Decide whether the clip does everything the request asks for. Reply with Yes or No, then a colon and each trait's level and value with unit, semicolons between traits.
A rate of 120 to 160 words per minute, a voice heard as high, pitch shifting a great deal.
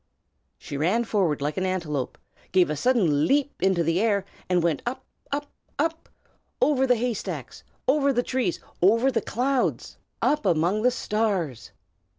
Yes: average, 155 wpm; high, 210 Hz; wide, 7.0 semitones